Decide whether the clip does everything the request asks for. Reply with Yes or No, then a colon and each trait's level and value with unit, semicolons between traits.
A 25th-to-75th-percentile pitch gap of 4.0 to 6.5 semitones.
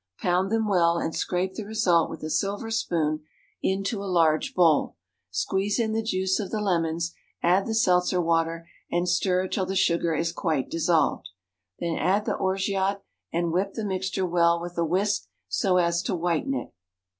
No: average, 2.7 semitones